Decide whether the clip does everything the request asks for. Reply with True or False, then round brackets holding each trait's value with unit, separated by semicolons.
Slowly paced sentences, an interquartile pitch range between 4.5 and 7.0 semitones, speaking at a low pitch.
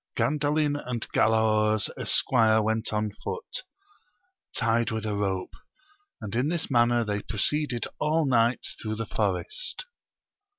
True (125 wpm; 5.1 semitones; 115 Hz)